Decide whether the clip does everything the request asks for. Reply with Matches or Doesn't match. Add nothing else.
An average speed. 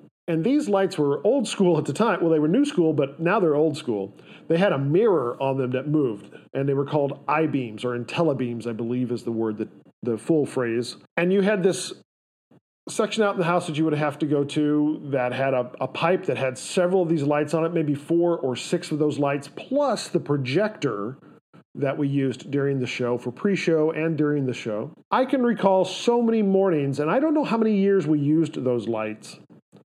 Doesn't match